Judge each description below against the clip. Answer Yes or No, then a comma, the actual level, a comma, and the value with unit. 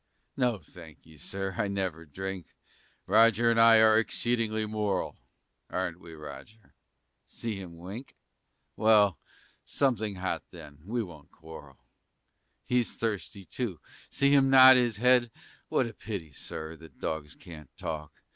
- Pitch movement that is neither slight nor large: No, wide, 5.8 semitones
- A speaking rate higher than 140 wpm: No, slow, 135 wpm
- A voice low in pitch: Yes, low, 100 Hz